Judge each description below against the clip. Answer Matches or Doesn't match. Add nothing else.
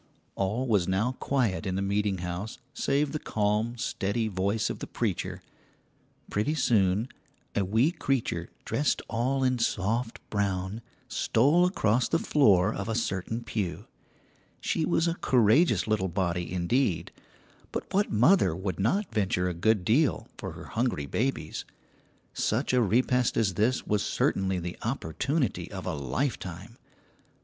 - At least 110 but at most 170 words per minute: Matches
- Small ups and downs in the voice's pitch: Doesn't match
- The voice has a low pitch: Matches